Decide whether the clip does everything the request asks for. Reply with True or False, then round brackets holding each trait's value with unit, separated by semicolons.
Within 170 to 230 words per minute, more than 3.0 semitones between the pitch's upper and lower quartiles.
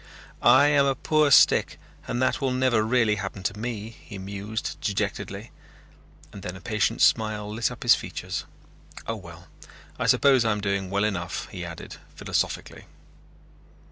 False (155 wpm; 3.6 semitones)